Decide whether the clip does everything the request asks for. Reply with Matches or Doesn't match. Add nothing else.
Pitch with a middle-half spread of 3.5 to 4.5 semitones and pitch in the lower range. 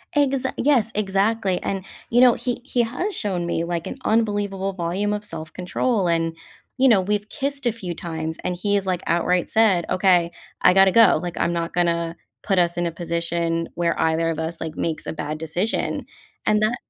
Doesn't match